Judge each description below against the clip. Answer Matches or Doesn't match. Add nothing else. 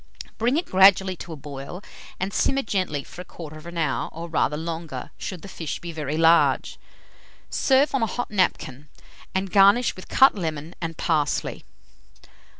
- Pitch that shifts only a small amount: Doesn't match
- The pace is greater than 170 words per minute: Doesn't match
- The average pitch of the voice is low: Doesn't match